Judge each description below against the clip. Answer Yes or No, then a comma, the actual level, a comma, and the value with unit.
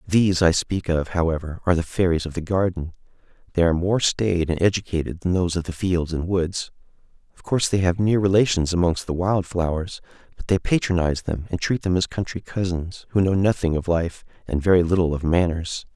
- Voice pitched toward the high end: No, very low, 90 Hz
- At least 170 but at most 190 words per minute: No, fast, 205 wpm